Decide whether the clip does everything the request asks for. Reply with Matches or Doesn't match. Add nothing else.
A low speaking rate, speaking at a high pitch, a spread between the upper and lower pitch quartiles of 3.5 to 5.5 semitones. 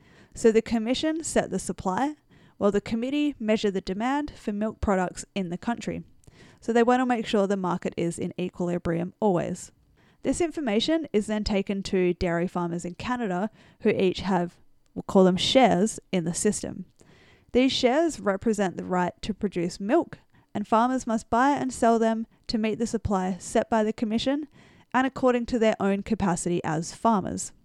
Doesn't match